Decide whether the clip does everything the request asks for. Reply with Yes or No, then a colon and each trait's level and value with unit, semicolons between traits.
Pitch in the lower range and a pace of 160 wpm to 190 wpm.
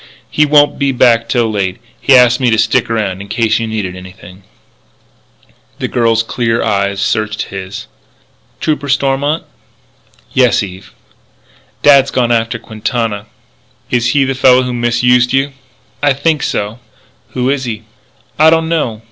No: low, 120 Hz; average, 150 wpm